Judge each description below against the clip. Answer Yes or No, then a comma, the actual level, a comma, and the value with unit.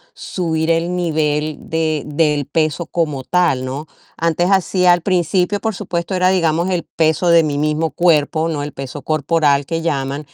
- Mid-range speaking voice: Yes, medium, 160 Hz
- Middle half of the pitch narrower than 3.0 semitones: Yes, narrow, 2.6 semitones